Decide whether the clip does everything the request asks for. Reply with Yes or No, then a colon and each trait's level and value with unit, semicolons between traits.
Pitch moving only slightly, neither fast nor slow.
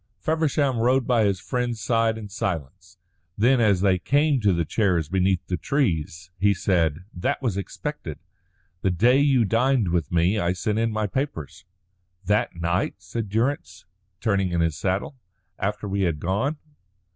No: average, 5.0 semitones; average, 160 wpm